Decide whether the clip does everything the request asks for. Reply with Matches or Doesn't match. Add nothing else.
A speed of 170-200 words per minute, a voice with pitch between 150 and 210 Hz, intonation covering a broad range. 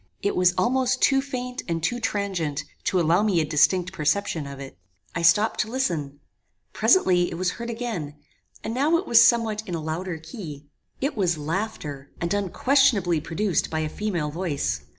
Matches